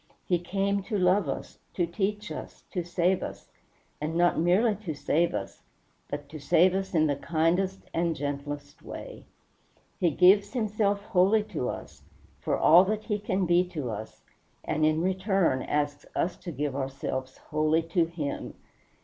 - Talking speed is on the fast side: No, average, 165 wpm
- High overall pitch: No, medium, 175 Hz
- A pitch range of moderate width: Yes, average, 4.2 semitones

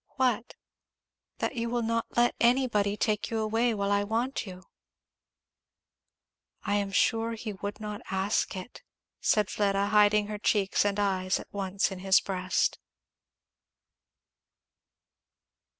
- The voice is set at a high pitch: Yes, high, 210 Hz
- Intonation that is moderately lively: No, narrow, 2.3 semitones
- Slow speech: Yes, slow, 130 wpm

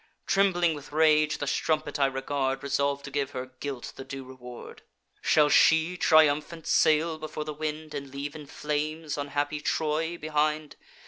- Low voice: No, medium, 150 Hz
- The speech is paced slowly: No, average, 155 wpm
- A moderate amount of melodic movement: No, narrow, 1.9 semitones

